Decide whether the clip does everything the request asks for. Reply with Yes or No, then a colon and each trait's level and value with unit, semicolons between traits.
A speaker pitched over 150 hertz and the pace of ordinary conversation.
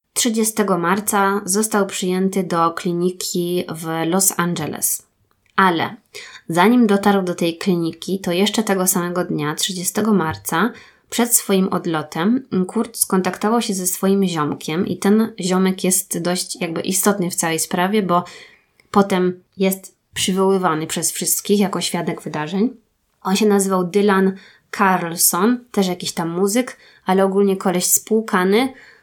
Yes: high, 190 Hz; average, 130 wpm